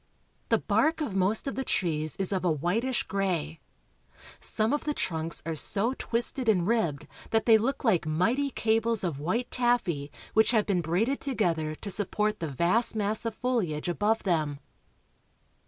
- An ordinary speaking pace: Yes, average, 170 wpm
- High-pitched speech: Yes, high, 205 Hz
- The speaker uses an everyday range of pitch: No, wide, 5.7 semitones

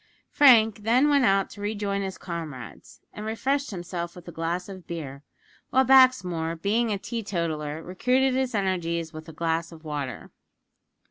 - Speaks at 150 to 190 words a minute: Yes, average, 155 wpm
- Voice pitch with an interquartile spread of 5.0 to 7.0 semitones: Yes, wide, 5.4 semitones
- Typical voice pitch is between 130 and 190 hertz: Yes, medium, 185 Hz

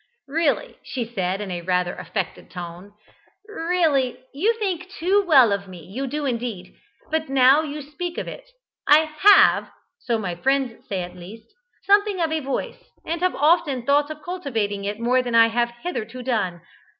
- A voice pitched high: Yes, very high, 260 Hz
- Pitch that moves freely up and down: Yes, wide, 7.7 semitones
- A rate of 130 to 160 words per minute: No, average, 175 wpm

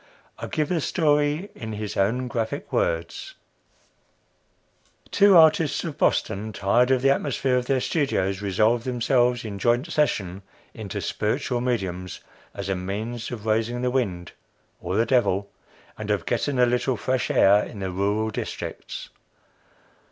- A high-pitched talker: No, low, 120 Hz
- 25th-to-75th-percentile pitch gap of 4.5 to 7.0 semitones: Yes, average, 5.0 semitones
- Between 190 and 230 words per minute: No, average, 145 wpm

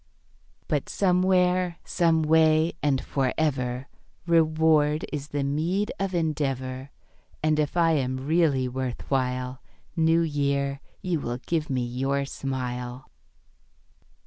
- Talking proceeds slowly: Yes, slow, 120 wpm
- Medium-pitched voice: Yes, medium, 145 Hz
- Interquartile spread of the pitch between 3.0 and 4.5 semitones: Yes, average, 3.8 semitones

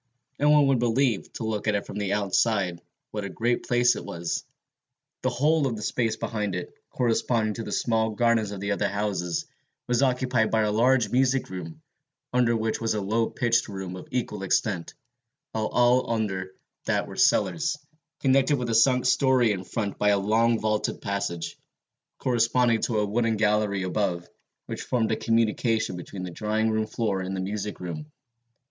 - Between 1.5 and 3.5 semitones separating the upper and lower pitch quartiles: Yes, average, 3.2 semitones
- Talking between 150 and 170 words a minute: No, average, 180 wpm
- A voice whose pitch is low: Yes, low, 110 Hz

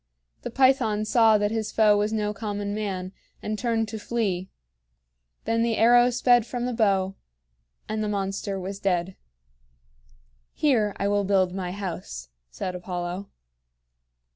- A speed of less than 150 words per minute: Yes, average, 140 wpm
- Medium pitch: No, high, 205 Hz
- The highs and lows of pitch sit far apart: No, average, 2.8 semitones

